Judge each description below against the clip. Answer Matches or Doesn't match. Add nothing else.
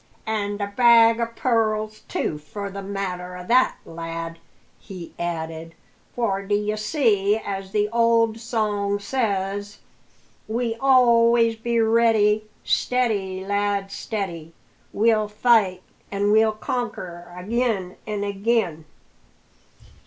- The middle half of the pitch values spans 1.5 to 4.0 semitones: Matches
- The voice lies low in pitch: Doesn't match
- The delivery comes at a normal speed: Doesn't match